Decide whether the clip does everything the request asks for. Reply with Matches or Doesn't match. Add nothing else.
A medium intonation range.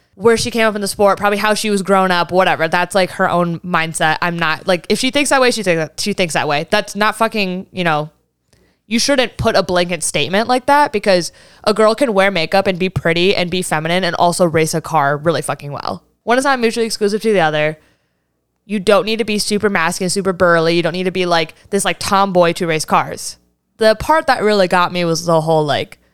Matches